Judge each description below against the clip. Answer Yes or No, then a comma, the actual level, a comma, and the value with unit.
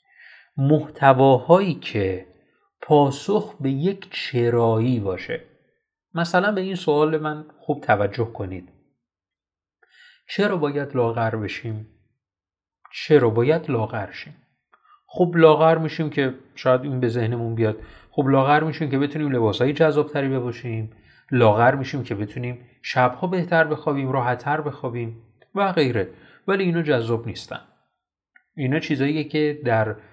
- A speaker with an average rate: Yes, average, 120 wpm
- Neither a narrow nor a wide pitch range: Yes, average, 5.0 semitones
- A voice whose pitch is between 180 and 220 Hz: No, medium, 140 Hz